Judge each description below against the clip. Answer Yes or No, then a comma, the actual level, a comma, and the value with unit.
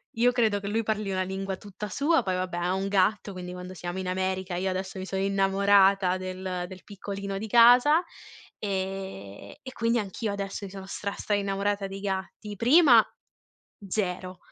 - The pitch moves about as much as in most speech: No, narrow, 1.9 semitones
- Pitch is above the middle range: Yes, high, 195 Hz